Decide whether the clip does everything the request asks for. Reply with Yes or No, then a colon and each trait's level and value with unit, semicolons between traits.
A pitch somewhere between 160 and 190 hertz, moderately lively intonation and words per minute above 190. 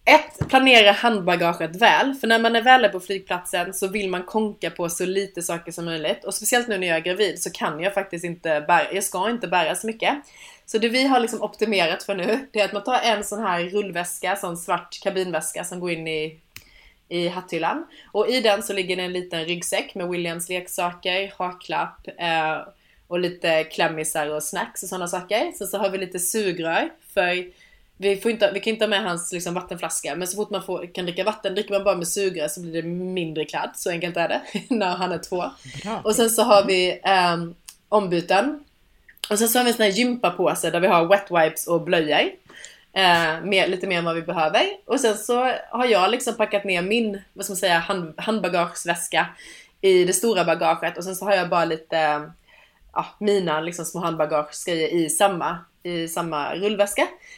Yes: medium, 185 Hz; average, 3.5 semitones; fast, 205 wpm